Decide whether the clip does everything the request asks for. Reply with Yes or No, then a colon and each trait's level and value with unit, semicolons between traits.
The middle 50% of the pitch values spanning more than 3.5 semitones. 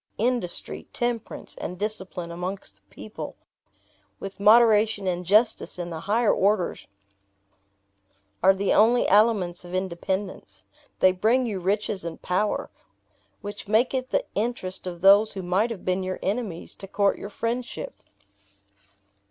No: average, 3.2 semitones